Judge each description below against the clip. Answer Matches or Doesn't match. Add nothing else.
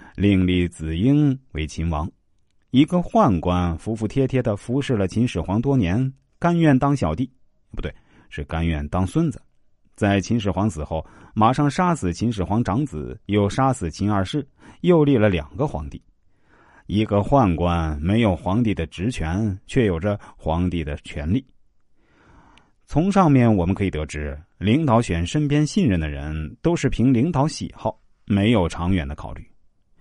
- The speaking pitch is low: Matches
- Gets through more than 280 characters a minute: Doesn't match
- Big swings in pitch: Matches